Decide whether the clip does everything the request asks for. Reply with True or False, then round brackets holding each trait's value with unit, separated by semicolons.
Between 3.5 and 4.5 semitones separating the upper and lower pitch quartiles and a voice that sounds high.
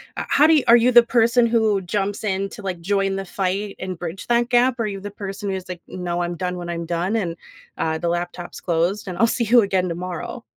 True (4.2 semitones; 195 Hz)